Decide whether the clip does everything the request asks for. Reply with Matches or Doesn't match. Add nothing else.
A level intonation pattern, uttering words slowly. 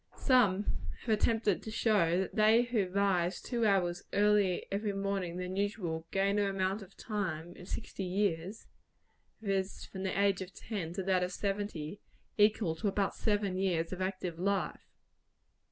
Doesn't match